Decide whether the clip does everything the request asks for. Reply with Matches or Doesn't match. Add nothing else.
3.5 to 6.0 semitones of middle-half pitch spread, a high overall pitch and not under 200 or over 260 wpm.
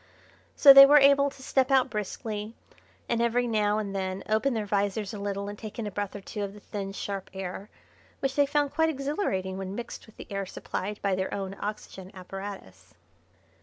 Matches